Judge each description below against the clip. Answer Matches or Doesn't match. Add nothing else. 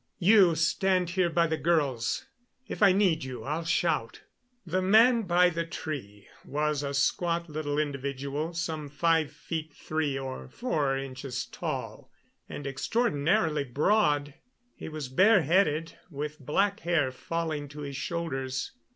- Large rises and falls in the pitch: Doesn't match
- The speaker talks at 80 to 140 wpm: Matches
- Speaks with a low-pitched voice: Doesn't match